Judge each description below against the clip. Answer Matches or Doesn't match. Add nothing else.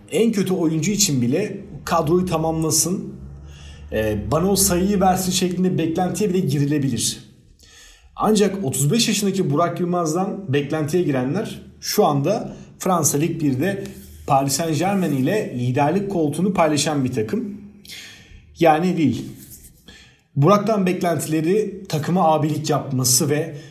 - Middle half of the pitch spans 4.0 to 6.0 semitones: Matches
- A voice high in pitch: Doesn't match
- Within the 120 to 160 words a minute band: Doesn't match